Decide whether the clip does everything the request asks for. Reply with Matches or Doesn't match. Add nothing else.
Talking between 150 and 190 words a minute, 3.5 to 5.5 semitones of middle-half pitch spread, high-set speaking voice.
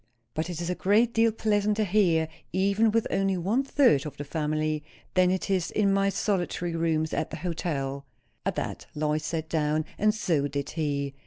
Doesn't match